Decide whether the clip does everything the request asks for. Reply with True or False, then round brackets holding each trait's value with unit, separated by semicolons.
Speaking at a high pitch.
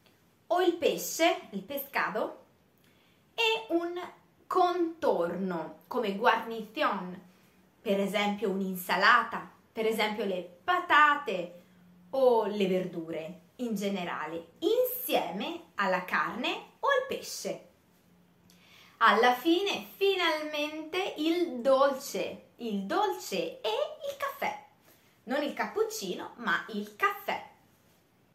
True (255 Hz)